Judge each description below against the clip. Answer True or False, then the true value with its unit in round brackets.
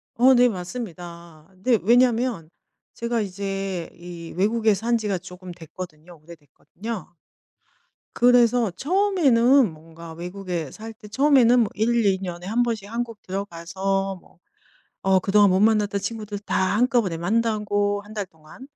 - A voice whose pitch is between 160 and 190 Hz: False (200 Hz)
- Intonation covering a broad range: False (4.6 semitones)